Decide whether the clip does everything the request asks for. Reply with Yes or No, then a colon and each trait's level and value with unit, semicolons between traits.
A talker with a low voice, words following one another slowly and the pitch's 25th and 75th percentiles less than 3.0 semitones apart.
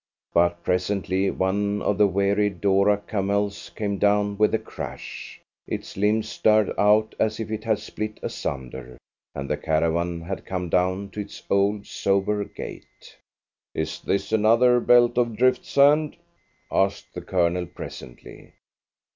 No: low, 100 Hz; average, 145 wpm; narrow, 2.6 semitones